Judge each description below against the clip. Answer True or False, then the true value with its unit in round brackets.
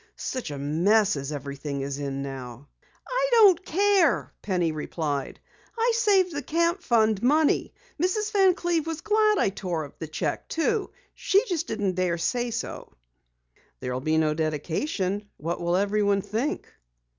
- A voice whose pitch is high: True (205 Hz)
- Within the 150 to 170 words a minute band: True (155 wpm)